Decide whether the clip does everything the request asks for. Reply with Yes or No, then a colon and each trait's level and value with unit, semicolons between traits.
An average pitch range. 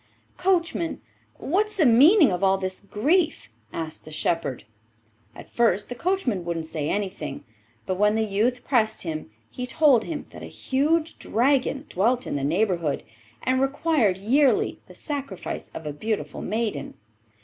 No: wide, 7.5 semitones